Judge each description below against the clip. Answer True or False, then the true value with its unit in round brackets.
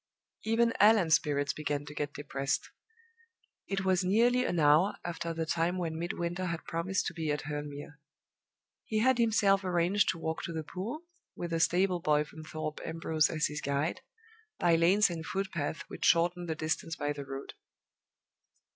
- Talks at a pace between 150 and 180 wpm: True (175 wpm)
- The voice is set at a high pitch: False (165 Hz)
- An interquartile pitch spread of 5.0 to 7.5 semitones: False (3.6 semitones)